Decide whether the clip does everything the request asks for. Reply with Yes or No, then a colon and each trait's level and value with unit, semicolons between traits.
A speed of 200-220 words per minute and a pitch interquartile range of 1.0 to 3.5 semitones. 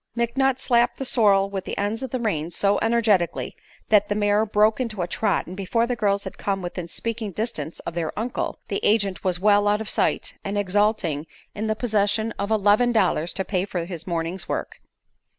Yes: fast, 205 wpm; average, 3.0 semitones